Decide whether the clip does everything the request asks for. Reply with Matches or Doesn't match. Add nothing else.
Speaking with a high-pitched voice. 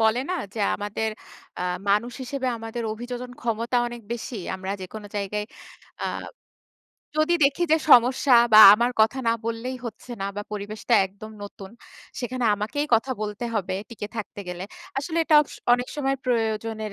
Matches